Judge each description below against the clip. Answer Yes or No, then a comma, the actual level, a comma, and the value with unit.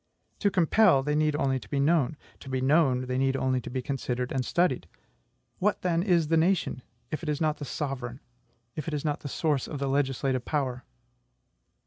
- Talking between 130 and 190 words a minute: No, average, 200 wpm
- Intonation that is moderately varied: Yes, average, 3.4 semitones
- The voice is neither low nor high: Yes, medium, 145 Hz